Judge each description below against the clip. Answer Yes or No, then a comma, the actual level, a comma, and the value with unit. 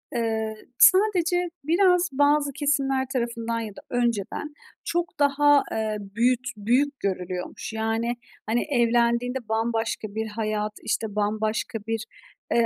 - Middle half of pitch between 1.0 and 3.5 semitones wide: No, average, 4.4 semitones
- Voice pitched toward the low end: No, high, 235 Hz